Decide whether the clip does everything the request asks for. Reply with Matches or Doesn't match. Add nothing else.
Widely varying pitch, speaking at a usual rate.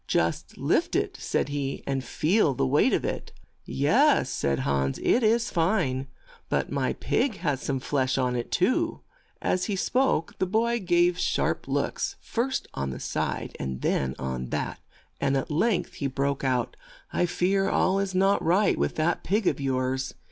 Matches